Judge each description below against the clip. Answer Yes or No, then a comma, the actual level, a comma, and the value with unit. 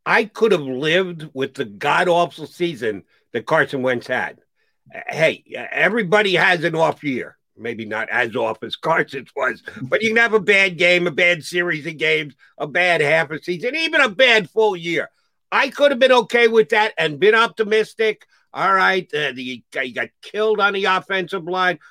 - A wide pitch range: Yes, wide, 5.8 semitones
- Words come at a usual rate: Yes, average, 190 wpm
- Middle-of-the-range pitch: Yes, medium, 180 Hz